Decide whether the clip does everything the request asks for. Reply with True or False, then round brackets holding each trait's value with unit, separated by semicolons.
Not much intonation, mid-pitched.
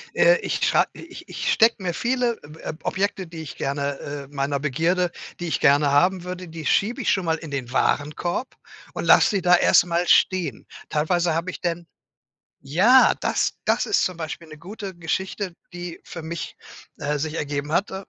False (3.9 semitones; 170 Hz)